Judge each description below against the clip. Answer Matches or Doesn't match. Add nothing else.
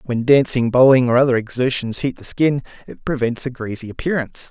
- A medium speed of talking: Matches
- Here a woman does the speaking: Doesn't match